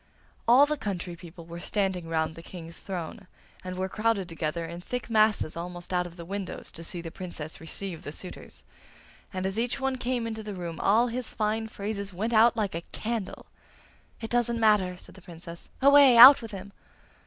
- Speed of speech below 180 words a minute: No, average, 195 wpm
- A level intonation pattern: No, average, 4.6 semitones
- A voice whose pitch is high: Yes, high, 195 Hz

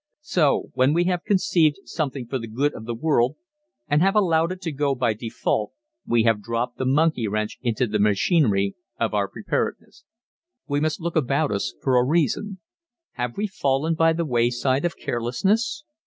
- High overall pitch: No, low, 135 Hz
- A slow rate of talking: No, average, 180 wpm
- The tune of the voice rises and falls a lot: Yes, wide, 5.8 semitones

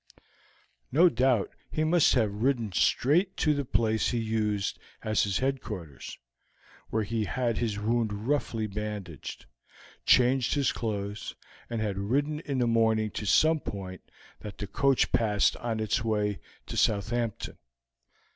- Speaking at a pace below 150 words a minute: Yes, average, 140 wpm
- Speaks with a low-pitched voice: Yes, low, 110 Hz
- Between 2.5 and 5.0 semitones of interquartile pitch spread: Yes, average, 3.8 semitones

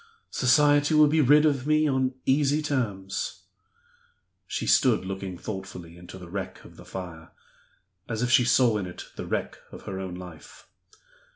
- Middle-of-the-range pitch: No, low, 115 Hz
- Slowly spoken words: No, average, 165 wpm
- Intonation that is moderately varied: No, wide, 7.4 semitones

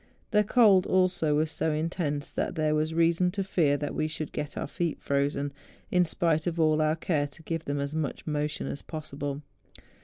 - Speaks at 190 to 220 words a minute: Yes, average, 195 wpm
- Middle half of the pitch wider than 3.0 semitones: No, narrow, 2.4 semitones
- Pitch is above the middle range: No, medium, 155 Hz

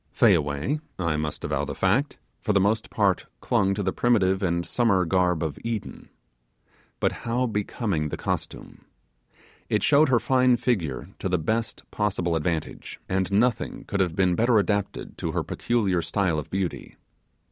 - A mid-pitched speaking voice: No, very low, 95 Hz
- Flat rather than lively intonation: No, average, 4.9 semitones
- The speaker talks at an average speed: Yes, average, 160 wpm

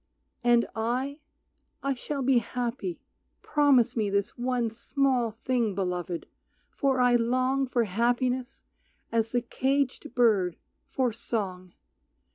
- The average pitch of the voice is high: Yes, high, 240 Hz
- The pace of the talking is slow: Yes, slow, 115 wpm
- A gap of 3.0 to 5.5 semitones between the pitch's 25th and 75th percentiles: No, narrow, 2.6 semitones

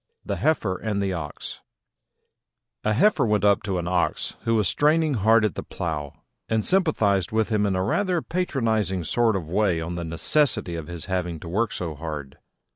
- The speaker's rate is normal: Yes, average, 190 wpm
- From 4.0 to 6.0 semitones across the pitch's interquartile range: Yes, average, 4.7 semitones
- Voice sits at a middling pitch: No, low, 100 Hz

